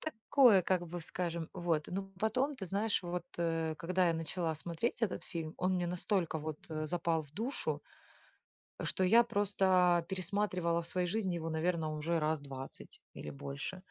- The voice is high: No, medium, 175 Hz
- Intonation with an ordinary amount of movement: Yes, average, 3.0 semitones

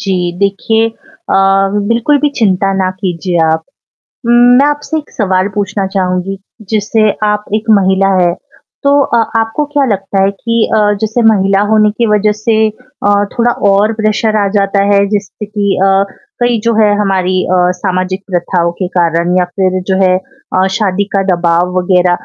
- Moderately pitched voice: No, high, 200 Hz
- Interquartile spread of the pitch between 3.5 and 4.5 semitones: No, average, 3.1 semitones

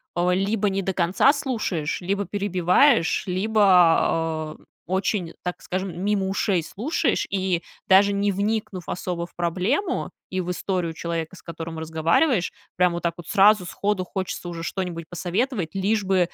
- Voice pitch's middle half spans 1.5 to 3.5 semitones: Yes, average, 2.8 semitones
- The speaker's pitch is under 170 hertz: No, medium, 185 Hz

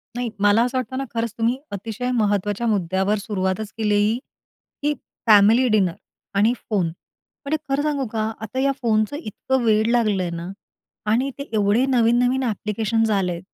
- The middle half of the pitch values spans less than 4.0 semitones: Yes, average, 3.3 semitones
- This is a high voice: Yes, high, 220 Hz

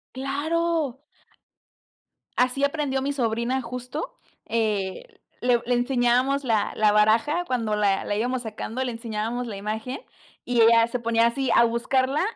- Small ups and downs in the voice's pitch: No, average, 3.0 semitones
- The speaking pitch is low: No, high, 245 Hz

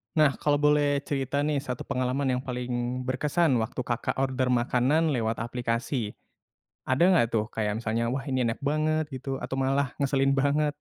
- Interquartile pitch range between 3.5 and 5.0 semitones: No, average, 2.8 semitones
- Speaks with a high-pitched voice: No, low, 130 Hz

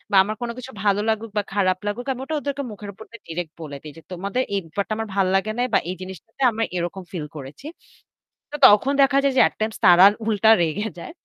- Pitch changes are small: No, average, 3.7 semitones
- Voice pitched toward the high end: Yes, high, 205 Hz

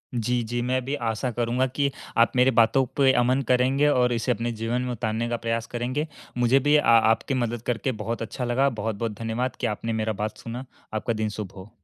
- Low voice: Yes, low, 120 Hz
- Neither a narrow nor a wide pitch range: No, narrow, 2.2 semitones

